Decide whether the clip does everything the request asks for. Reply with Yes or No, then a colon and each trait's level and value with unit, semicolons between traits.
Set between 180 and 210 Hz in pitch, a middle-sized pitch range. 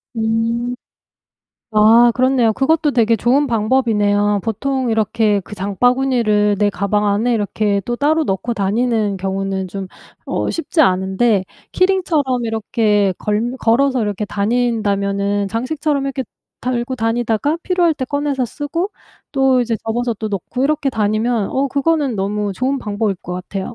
No: high, 230 Hz; average, 4.3 semitones